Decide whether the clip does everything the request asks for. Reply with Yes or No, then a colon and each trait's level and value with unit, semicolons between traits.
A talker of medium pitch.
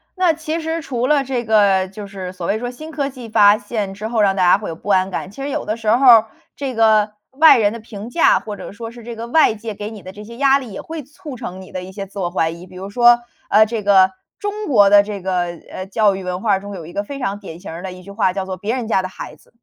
No: high, 210 Hz